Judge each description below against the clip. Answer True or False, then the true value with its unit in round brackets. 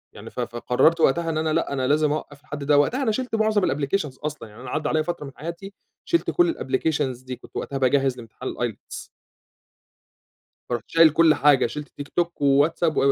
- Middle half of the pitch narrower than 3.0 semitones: False (4.0 semitones)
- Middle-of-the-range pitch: True (150 Hz)